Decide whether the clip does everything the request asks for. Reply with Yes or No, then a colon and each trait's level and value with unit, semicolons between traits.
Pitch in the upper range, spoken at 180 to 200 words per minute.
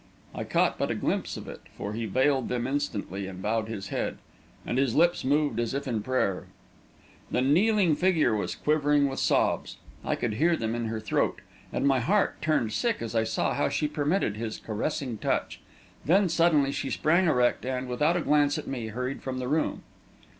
No: low, 130 Hz; average, 195 wpm